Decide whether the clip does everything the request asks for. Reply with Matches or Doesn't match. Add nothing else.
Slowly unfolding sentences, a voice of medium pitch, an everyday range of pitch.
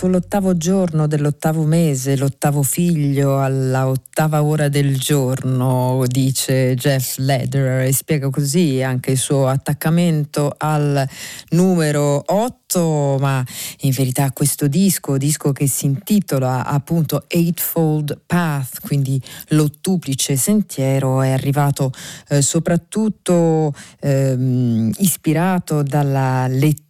Matches